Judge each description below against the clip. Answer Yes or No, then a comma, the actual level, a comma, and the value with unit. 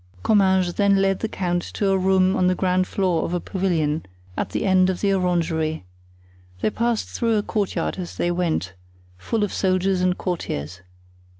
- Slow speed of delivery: No, average, 180 wpm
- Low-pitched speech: No, medium, 185 Hz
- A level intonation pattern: Yes, narrow, 1.9 semitones